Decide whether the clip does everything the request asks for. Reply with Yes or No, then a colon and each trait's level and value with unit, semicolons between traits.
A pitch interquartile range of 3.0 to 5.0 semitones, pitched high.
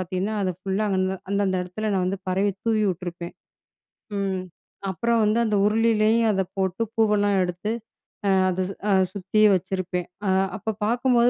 No: narrow, 2.6 semitones; high, 200 Hz